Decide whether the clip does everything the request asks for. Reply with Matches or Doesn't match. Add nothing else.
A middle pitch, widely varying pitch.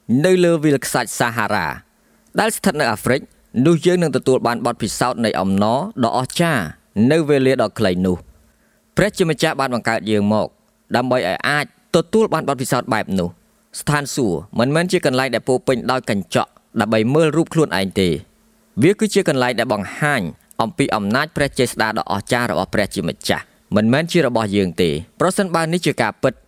Doesn't match